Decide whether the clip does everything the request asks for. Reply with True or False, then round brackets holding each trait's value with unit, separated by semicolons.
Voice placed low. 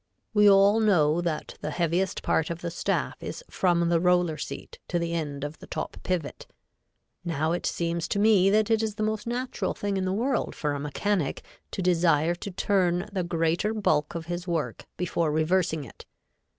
False (175 Hz)